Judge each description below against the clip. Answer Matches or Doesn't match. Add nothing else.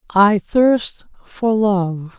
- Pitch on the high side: Matches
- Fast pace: Doesn't match